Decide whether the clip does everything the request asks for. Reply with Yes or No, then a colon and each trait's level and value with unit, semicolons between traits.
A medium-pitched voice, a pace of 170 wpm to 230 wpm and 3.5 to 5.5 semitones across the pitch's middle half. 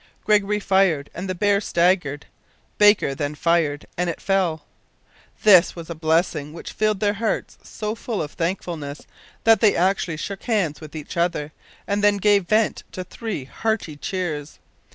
No: medium, 180 Hz; average, 160 wpm; average, 4.6 semitones